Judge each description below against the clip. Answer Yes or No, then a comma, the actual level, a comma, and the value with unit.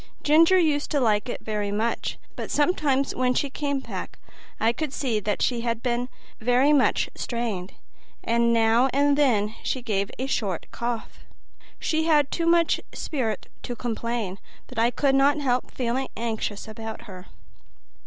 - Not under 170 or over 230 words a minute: No, average, 160 wpm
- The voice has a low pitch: No, high, 245 Hz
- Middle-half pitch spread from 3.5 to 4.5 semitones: Yes, average, 4.1 semitones